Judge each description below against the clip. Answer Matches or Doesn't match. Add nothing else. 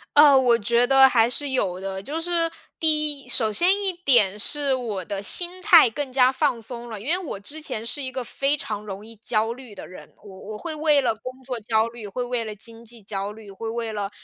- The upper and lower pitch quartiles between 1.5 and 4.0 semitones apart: Doesn't match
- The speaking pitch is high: Matches